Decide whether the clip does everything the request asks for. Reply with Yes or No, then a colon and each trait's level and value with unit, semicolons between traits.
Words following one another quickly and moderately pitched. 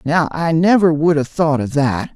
Yes: fast, 225 wpm; medium, 155 Hz